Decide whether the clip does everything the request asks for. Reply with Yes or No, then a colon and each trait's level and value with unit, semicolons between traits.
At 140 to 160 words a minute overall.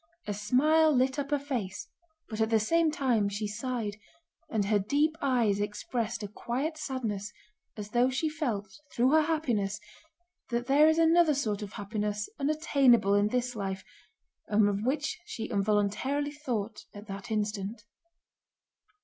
Yes: average, 150 wpm